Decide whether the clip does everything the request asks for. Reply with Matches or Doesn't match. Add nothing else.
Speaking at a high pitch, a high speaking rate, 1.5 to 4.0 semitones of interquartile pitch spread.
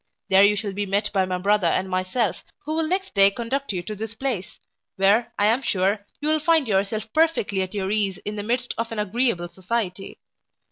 Matches